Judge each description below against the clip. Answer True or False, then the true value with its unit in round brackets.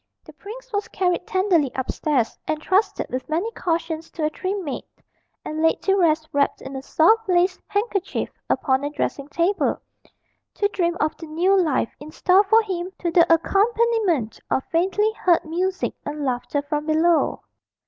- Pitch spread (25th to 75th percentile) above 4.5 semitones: False (4.1 semitones)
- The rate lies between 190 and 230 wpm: False (165 wpm)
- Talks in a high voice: True (340 Hz)